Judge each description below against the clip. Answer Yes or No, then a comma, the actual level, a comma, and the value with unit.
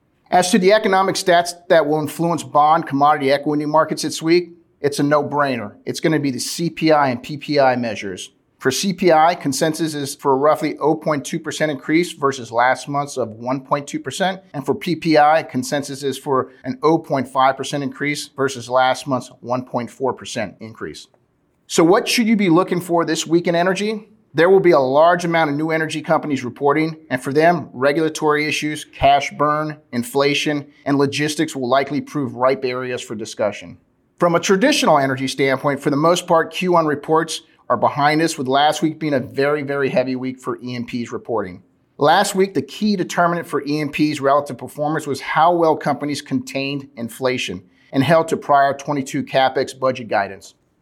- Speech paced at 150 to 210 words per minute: Yes, average, 170 wpm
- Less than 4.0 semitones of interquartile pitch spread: Yes, average, 3.3 semitones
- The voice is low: No, medium, 145 Hz